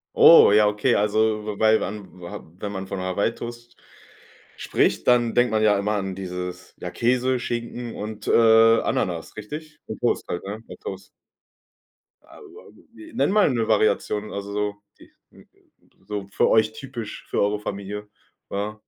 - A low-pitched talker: Yes, low, 105 Hz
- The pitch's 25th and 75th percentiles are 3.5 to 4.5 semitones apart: No, narrow, 2.6 semitones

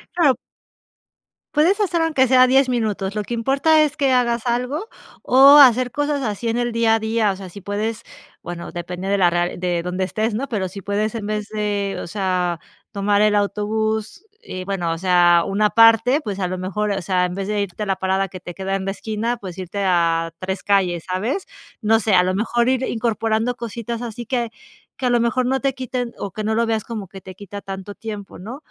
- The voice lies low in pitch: No, high, 210 Hz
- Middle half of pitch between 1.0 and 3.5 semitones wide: No, average, 4.0 semitones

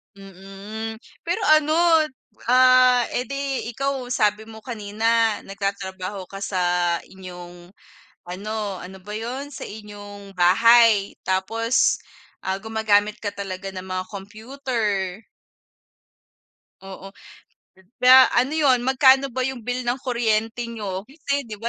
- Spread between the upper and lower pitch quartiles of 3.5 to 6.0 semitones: Yes, average, 4.3 semitones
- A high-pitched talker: Yes, high, 220 Hz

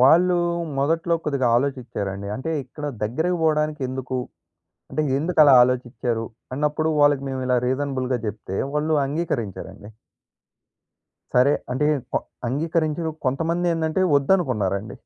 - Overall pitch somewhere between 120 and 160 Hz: Yes, medium, 140 Hz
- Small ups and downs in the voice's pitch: No, average, 4.0 semitones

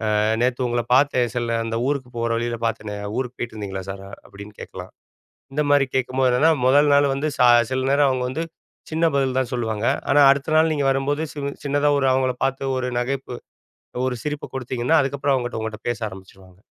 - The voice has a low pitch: Yes, low, 130 Hz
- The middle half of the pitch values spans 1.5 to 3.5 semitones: Yes, average, 3.0 semitones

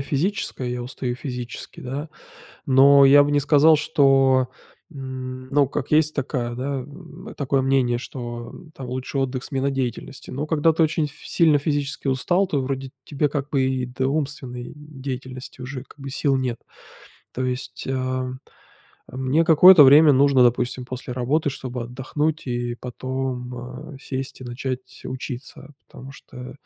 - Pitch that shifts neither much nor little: No, narrow, 2.2 semitones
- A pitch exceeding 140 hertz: No, low, 135 Hz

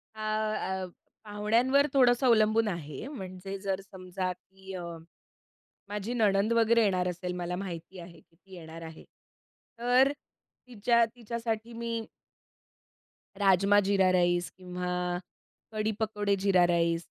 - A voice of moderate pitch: No, high, 195 Hz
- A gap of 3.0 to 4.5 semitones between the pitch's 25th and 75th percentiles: Yes, average, 3.7 semitones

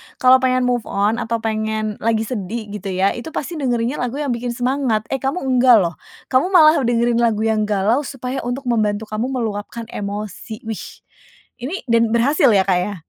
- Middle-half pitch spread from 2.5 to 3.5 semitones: Yes, average, 3.1 semitones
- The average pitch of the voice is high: Yes, high, 230 Hz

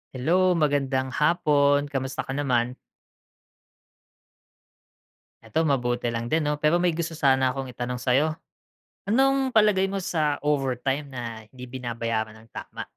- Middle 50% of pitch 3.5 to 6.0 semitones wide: Yes, average, 4.1 semitones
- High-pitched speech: No, medium, 140 Hz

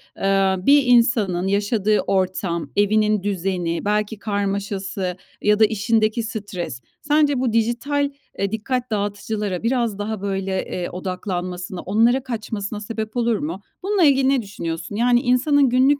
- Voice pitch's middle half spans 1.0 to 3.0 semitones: No, average, 3.6 semitones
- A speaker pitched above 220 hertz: No, high, 210 Hz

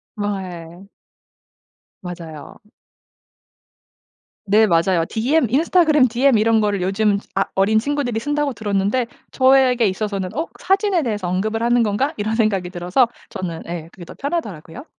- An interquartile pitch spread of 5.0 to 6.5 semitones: Yes, wide, 5.5 semitones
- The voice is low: No, high, 215 Hz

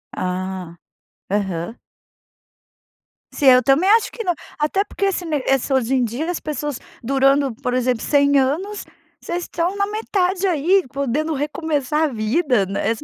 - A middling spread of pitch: No, wide, 5.8 semitones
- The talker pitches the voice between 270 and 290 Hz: Yes, very high, 280 Hz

